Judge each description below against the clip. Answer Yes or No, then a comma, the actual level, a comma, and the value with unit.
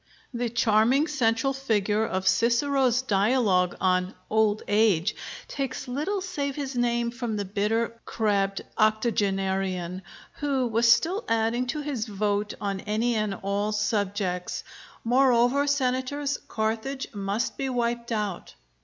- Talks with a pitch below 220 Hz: No, high, 225 Hz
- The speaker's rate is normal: No, slow, 125 wpm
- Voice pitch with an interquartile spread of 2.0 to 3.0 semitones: No, average, 4.0 semitones